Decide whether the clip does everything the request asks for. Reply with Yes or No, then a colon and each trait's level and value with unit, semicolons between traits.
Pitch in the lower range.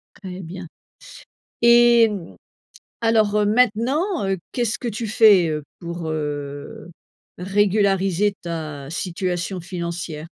No: high, 190 Hz